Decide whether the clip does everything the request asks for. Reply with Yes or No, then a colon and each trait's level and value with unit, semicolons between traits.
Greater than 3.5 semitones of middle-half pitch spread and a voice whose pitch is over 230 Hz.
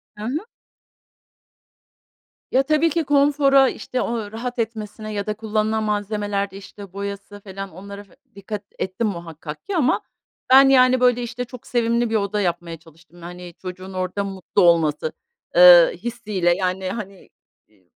No: average, 4.3 semitones; high, 205 Hz